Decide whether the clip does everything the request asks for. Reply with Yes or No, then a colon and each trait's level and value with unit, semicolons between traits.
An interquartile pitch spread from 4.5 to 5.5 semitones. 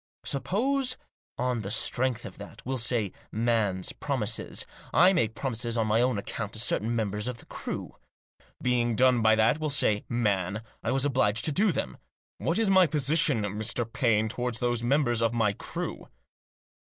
No: average, 3.4 semitones